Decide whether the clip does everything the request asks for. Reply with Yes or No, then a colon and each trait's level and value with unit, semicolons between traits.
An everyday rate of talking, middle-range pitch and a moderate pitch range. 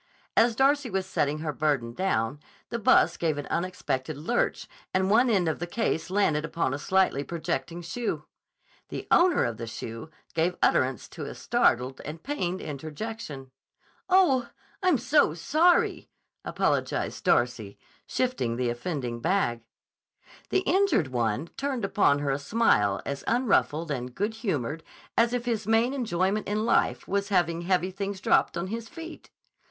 No: average, 155 wpm; medium, 180 Hz; wide, 8.1 semitones